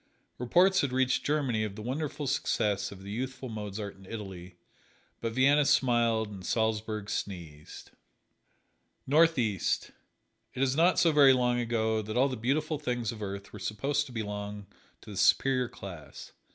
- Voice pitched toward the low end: Yes, low, 115 Hz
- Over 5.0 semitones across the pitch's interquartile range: No, average, 4.6 semitones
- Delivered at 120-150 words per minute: No, average, 160 wpm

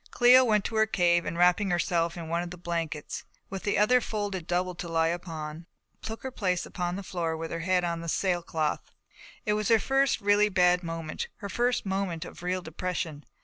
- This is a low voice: No, medium, 180 Hz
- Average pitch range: Yes, average, 3.3 semitones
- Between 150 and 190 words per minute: No, fast, 205 wpm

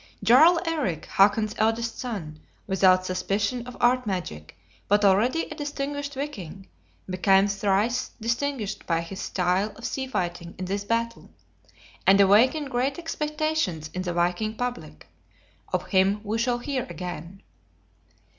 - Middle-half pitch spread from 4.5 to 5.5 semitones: Yes, average, 5.2 semitones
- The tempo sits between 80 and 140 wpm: Yes, slow, 135 wpm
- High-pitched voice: Yes, high, 210 Hz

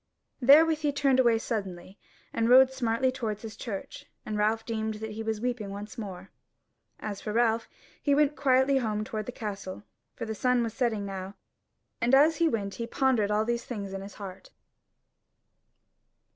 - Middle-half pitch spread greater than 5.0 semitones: No, average, 3.5 semitones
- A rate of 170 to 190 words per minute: Yes, average, 175 wpm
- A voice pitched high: Yes, high, 225 Hz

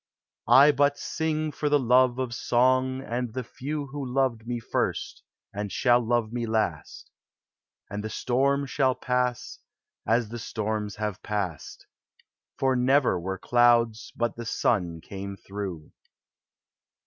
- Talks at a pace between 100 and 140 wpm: Yes, slow, 135 wpm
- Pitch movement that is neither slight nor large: Yes, average, 3.5 semitones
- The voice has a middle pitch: No, low, 120 Hz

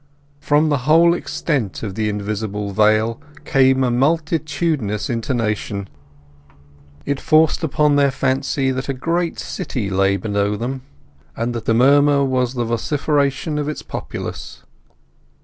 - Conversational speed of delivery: No, slow, 130 wpm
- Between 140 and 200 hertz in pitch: No, low, 130 Hz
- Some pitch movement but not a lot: Yes, average, 5.0 semitones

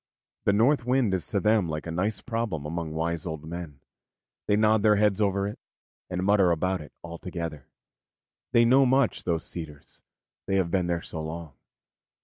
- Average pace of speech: Yes, average, 180 wpm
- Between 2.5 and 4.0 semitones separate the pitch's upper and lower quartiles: No, average, 4.4 semitones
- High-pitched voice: No, very low, 90 Hz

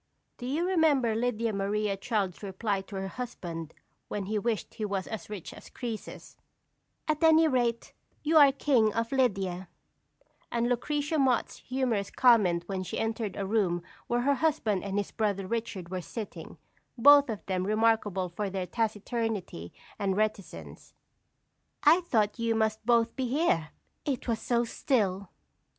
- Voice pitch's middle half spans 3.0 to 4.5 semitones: Yes, average, 4.0 semitones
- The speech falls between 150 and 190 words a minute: Yes, average, 155 wpm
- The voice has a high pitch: Yes, high, 220 Hz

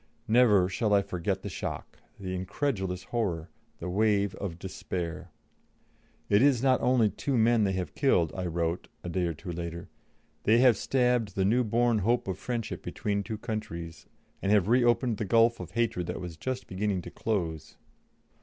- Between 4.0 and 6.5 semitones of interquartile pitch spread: Yes, average, 4.5 semitones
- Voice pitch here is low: Yes, low, 100 Hz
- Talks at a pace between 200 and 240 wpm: No, average, 175 wpm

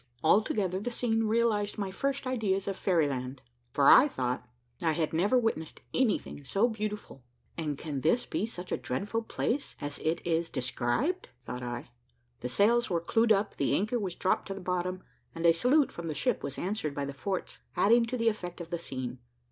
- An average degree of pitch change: No, wide, 6.4 semitones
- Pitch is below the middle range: No, medium, 185 Hz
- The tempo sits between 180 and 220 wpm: Yes, average, 195 wpm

